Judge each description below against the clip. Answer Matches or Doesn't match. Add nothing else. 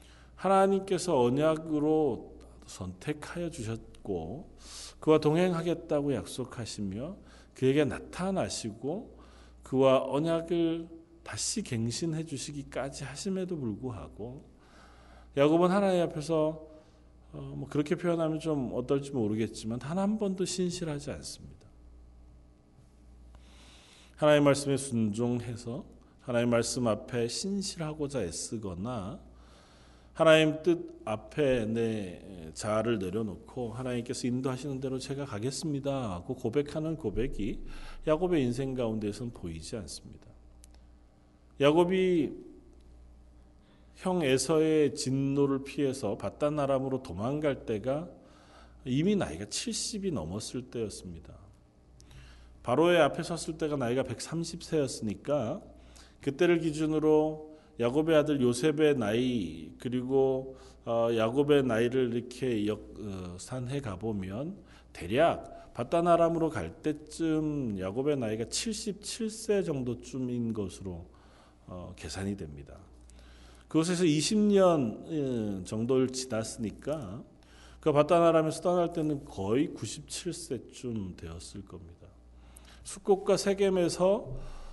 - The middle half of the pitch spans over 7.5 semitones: Matches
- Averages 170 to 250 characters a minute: Matches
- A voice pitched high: Doesn't match